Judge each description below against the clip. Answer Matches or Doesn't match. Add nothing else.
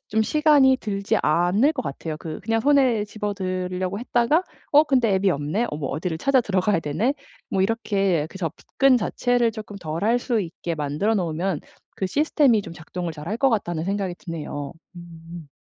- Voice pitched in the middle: Doesn't match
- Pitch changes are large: Matches